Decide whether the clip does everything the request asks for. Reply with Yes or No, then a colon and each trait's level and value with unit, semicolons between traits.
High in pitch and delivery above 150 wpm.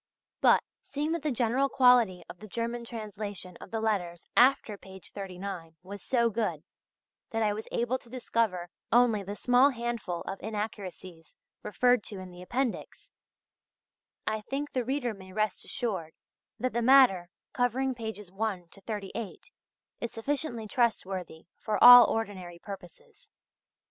No: high, 220 Hz; average, 145 wpm